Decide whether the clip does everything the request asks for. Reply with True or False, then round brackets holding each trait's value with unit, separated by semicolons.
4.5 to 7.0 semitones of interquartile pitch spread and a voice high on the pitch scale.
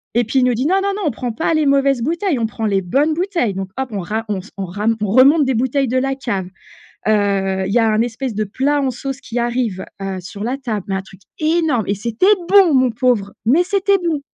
True (5.1 semitones; 245 Hz)